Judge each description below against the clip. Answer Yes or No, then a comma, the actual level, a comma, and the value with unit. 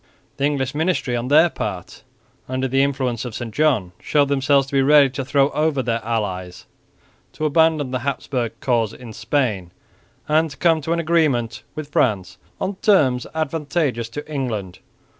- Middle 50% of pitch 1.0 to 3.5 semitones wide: No, average, 4.3 semitones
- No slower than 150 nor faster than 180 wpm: Yes, average, 165 wpm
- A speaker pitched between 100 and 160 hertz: Yes, low, 135 Hz